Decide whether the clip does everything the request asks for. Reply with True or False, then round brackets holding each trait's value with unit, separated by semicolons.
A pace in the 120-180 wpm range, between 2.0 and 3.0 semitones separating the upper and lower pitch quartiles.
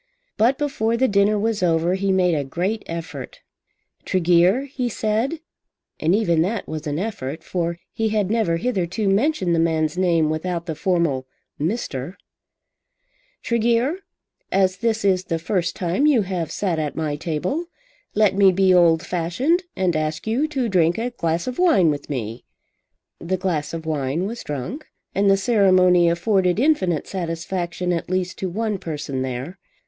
False (160 wpm; 4.7 semitones)